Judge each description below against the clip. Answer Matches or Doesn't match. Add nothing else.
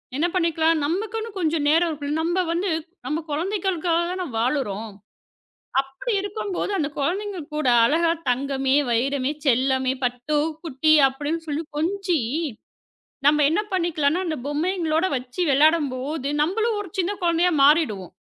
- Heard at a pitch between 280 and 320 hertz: Matches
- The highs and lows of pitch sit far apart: Doesn't match